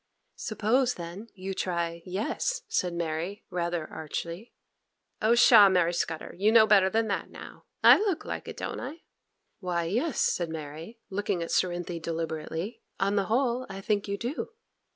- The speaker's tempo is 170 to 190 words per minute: No, average, 160 wpm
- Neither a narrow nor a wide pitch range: Yes, average, 4.6 semitones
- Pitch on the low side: No, high, 190 Hz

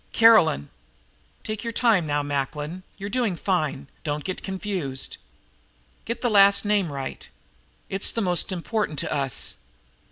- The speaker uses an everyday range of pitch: No, wide, 6.1 semitones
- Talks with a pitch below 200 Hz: Yes, medium, 185 Hz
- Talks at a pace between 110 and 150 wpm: Yes, slow, 135 wpm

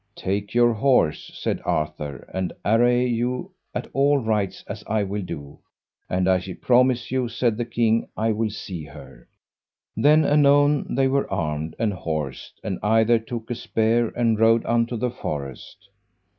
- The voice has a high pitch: No, low, 115 Hz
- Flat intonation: No, average, 4.4 semitones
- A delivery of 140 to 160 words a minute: Yes, average, 155 wpm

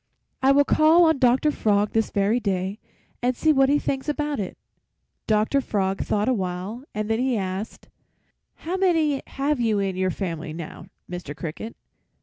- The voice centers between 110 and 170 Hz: No, high, 225 Hz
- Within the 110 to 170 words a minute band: Yes, average, 165 wpm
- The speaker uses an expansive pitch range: Yes, wide, 6.3 semitones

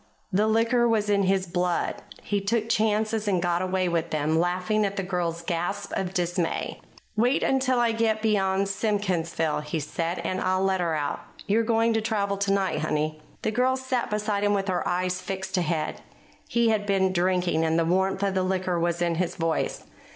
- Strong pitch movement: No, average, 3.4 semitones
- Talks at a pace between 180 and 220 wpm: Yes, average, 190 wpm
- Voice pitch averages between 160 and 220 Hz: Yes, high, 190 Hz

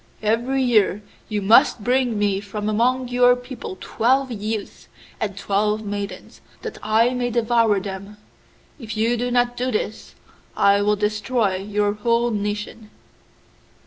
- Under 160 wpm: Yes, average, 140 wpm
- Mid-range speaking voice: No, high, 215 Hz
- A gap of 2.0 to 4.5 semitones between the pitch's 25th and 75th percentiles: Yes, average, 2.9 semitones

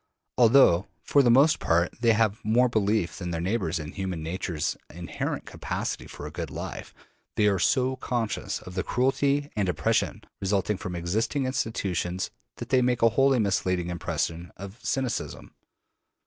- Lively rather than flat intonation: Yes, wide, 5.9 semitones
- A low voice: Yes, low, 105 Hz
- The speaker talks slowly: No, average, 160 wpm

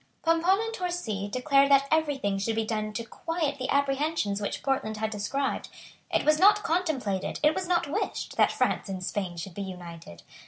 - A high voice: Yes, very high, 270 Hz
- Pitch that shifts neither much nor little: No, wide, 7.9 semitones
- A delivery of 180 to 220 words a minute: Yes, average, 190 wpm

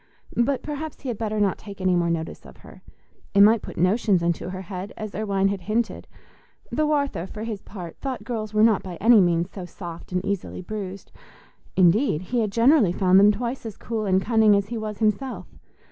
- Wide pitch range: No, average, 3.6 semitones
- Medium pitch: No, high, 205 Hz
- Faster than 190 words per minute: Yes, fast, 205 wpm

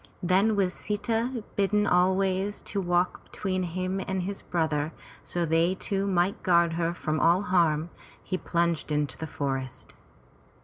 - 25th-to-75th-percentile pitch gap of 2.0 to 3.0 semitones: Yes, average, 2.7 semitones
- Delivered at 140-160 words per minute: Yes, average, 145 wpm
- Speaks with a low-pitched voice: No, medium, 180 Hz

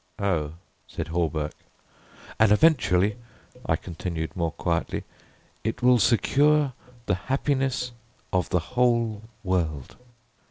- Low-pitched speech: Yes, low, 100 Hz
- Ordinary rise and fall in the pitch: No, wide, 7.0 semitones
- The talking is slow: Yes, slow, 105 wpm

